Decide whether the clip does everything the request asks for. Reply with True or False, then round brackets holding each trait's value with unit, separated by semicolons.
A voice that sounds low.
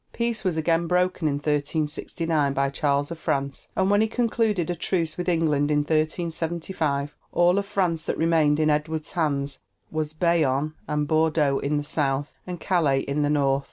False (155 Hz)